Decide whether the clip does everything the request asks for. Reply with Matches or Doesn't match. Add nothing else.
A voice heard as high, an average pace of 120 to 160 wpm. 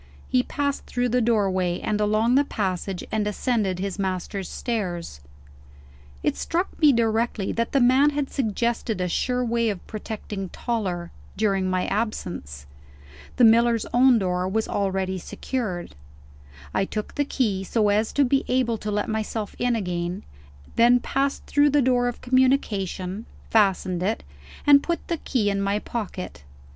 Matches